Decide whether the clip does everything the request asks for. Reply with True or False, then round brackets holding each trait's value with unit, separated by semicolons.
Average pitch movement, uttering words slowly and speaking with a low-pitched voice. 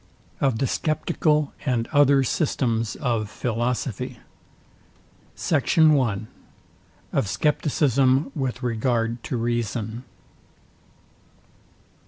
True (3.6 semitones; 80 wpm; 125 Hz)